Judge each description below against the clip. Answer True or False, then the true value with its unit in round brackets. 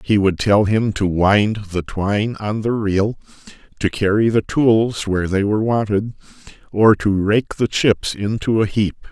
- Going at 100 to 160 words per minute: False (180 wpm)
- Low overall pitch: True (105 Hz)